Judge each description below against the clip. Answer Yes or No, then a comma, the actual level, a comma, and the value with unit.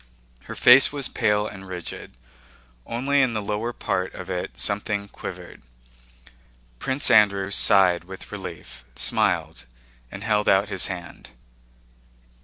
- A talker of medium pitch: No, low, 100 Hz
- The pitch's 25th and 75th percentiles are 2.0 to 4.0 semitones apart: Yes, average, 3.0 semitones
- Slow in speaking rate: Yes, slow, 125 wpm